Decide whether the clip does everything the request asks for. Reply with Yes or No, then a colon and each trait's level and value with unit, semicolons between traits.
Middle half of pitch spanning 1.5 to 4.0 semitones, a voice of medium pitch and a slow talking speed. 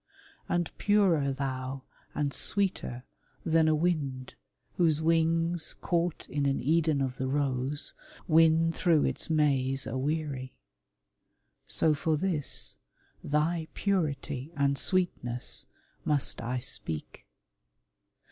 Yes: average, 3.5 semitones; medium, 150 Hz; slow, 105 wpm